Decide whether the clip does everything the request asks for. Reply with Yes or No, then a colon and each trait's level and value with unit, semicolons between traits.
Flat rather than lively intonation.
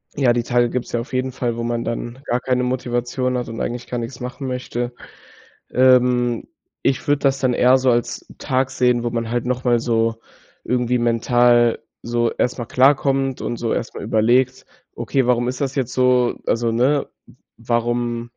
Yes: narrow, 1.3 semitones